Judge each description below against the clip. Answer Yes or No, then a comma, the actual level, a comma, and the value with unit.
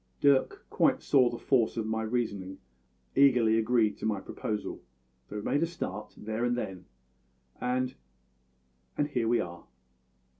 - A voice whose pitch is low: Yes, low, 115 Hz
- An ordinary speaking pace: Yes, average, 155 wpm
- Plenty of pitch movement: No, average, 3.0 semitones